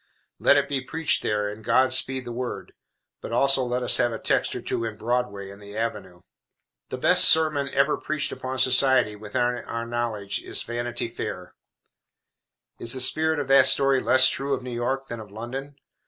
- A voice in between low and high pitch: No, low, 125 Hz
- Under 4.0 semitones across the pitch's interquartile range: Yes, average, 3.1 semitones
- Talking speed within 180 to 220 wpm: Yes, average, 190 wpm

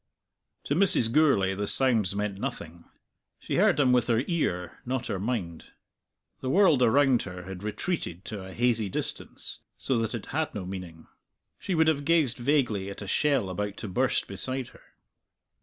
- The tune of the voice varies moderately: No, wide, 5.9 semitones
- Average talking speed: Yes, average, 175 wpm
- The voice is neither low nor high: No, low, 115 Hz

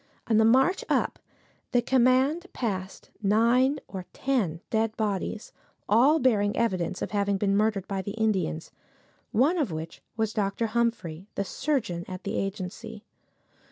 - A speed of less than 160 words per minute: Yes, average, 140 wpm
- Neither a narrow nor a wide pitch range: Yes, average, 3.9 semitones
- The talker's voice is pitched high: Yes, high, 215 Hz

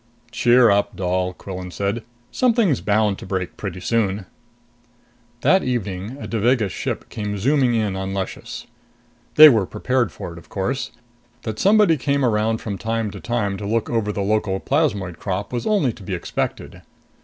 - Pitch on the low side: Yes, low, 110 Hz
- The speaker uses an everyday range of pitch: Yes, average, 4.1 semitones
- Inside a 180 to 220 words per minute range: No, average, 165 wpm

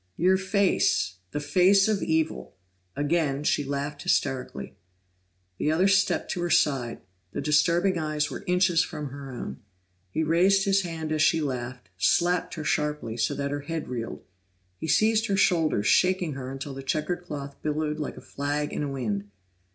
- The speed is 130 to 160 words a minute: No, average, 170 wpm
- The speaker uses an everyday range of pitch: Yes, average, 4.1 semitones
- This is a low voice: No, medium, 150 Hz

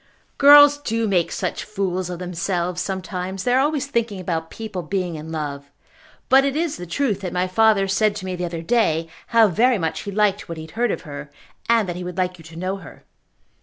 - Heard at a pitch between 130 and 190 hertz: Yes, medium, 185 Hz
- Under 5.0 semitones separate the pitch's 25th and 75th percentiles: Yes, average, 4.5 semitones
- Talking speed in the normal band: No, fast, 225 wpm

